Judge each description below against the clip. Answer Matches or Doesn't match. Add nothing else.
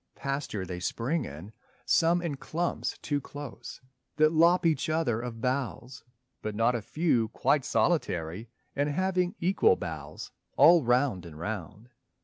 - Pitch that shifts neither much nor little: Doesn't match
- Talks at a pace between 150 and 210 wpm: Doesn't match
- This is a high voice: Doesn't match